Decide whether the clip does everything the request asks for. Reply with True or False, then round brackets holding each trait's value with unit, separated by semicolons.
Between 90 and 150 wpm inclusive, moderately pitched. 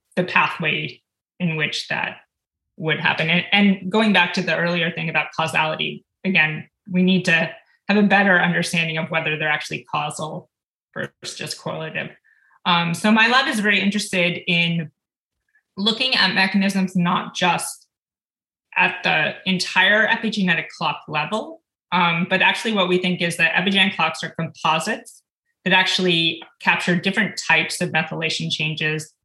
True (145 wpm; 180 Hz)